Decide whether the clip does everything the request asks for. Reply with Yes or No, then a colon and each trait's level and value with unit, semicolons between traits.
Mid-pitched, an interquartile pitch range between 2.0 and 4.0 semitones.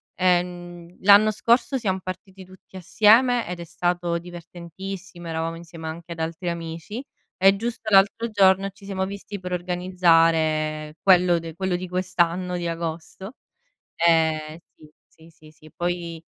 Yes: medium, 175 Hz; narrow, 2.5 semitones